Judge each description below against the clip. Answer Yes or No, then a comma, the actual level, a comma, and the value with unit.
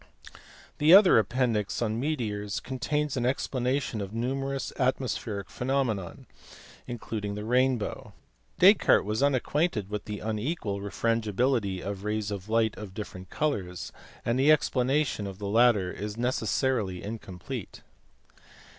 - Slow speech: Yes, slow, 120 wpm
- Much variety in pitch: No, average, 4.3 semitones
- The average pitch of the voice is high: No, low, 115 Hz